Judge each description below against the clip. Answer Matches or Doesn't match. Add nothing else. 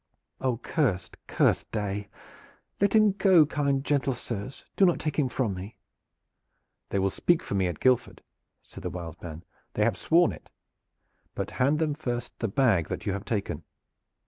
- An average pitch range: Doesn't match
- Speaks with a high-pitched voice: Doesn't match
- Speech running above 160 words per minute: Matches